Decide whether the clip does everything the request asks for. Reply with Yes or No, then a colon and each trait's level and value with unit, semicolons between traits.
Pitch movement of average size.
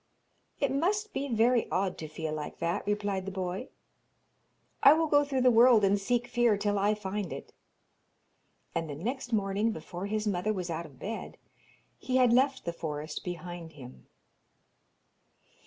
No: wide, 5.8 semitones